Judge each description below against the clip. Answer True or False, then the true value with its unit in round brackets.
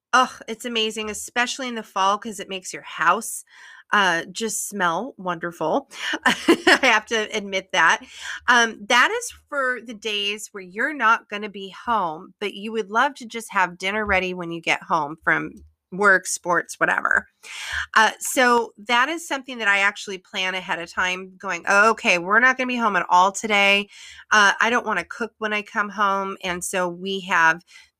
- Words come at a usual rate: True (190 wpm)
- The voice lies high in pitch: True (205 Hz)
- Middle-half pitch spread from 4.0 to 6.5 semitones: False (3.5 semitones)